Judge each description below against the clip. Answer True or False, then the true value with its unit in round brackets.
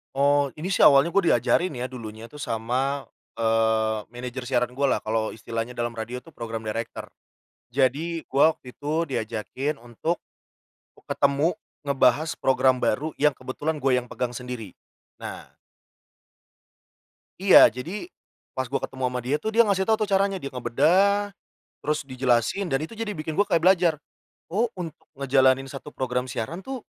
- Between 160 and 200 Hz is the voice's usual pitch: False (135 Hz)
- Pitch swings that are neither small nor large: True (5.0 semitones)